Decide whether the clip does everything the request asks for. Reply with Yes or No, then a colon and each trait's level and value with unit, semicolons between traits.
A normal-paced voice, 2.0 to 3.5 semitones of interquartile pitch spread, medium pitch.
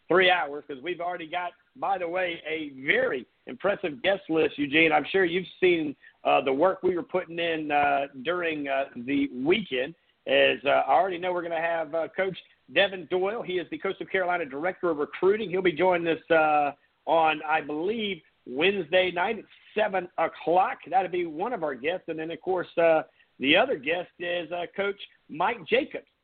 Yes: average, 190 wpm; average, 2.9 semitones; medium, 180 Hz